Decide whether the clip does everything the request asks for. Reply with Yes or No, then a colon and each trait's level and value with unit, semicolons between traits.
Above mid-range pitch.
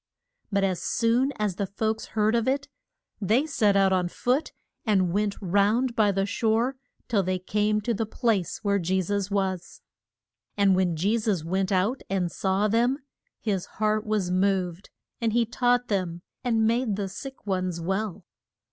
Yes: high, 205 Hz